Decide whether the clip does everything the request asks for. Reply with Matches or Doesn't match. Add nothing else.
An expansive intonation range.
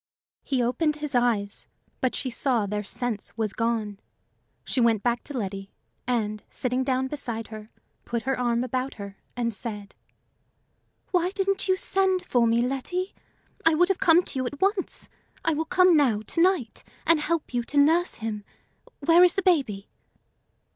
Matches